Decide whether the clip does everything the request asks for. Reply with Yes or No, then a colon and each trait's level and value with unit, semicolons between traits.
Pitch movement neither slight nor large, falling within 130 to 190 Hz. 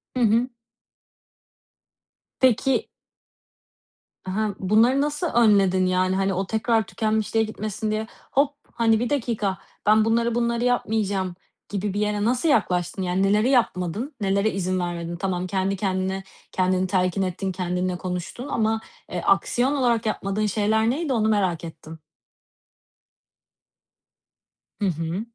No: average, 3.6 semitones; high, 205 Hz